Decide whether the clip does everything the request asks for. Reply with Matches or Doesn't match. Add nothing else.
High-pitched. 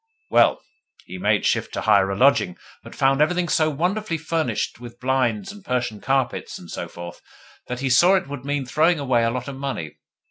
Doesn't match